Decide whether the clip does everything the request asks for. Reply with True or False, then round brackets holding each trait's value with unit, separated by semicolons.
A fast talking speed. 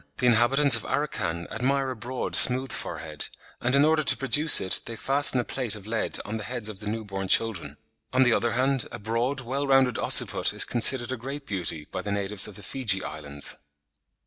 True (210 wpm)